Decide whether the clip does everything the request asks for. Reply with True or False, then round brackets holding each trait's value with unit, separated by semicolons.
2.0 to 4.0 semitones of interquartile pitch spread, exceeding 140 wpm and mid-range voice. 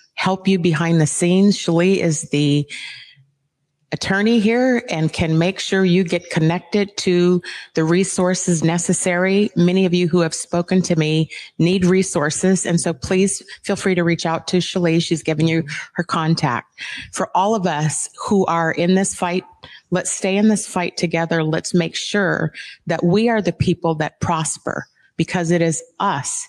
True (2.4 semitones; 170 wpm; 175 Hz)